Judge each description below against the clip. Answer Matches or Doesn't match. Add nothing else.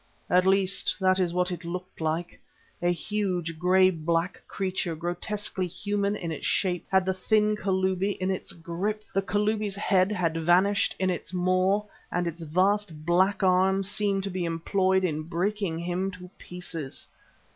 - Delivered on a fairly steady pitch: Matches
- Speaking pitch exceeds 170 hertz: Matches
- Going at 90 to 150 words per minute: Doesn't match